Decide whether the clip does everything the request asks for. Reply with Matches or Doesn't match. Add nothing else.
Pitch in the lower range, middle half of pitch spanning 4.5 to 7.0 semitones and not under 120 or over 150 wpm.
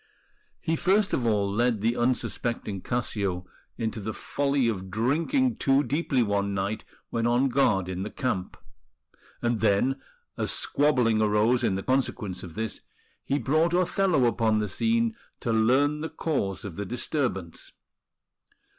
Matches